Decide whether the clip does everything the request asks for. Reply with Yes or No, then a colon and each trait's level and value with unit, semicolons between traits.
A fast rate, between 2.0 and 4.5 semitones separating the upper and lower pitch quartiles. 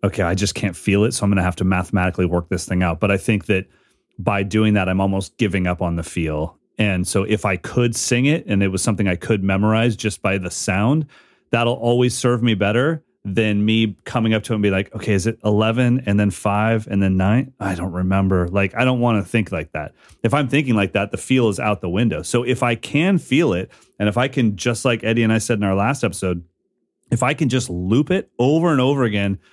Yes: fast, 250 wpm; average, 3.7 semitones